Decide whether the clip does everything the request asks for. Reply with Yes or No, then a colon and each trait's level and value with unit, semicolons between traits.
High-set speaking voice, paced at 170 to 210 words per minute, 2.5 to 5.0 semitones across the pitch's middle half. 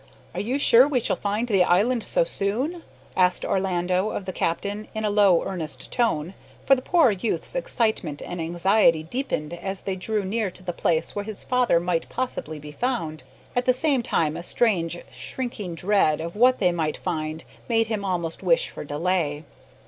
No: high, 195 Hz; average, 185 wpm; wide, 5.6 semitones